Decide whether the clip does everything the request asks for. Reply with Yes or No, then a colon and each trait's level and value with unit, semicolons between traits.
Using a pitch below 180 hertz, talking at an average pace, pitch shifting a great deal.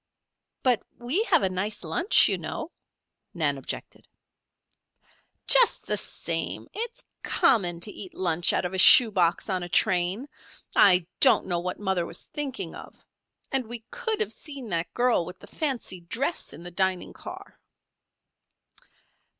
No: high, 190 Hz; average, 150 wpm; wide, 6.7 semitones